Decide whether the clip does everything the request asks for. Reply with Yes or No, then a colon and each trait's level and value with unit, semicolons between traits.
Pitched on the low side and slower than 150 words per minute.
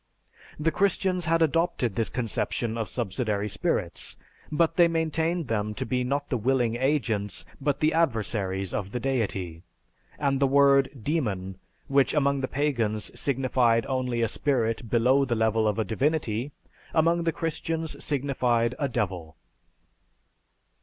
Yes: low, 130 Hz; average, 140 wpm